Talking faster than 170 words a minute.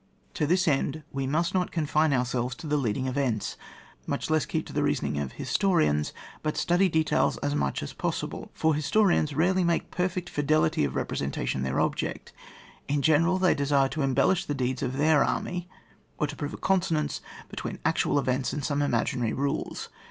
Yes: average, 190 wpm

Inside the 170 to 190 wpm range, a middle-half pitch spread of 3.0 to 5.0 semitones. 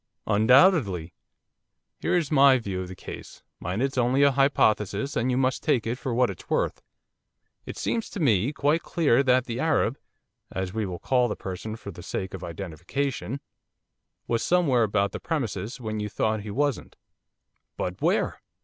No: average, 180 wpm; wide, 5.4 semitones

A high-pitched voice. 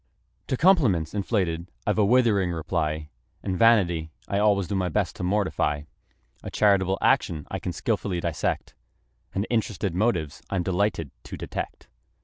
No: very low, 95 Hz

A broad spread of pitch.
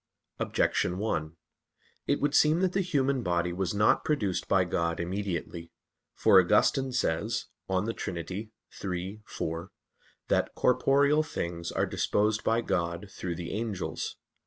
Yes: wide, 6.0 semitones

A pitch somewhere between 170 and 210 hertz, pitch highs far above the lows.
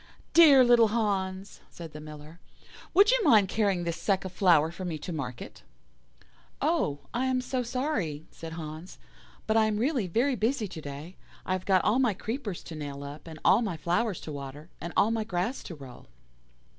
Yes: high, 190 Hz; wide, 6.5 semitones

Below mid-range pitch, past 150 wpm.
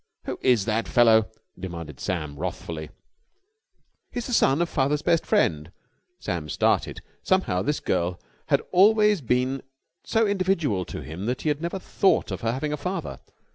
Yes: low, 130 Hz; average, 160 wpm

